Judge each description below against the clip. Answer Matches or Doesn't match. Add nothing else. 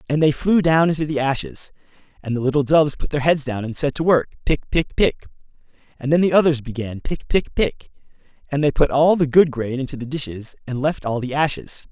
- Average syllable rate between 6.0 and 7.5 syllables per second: Doesn't match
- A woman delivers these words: Doesn't match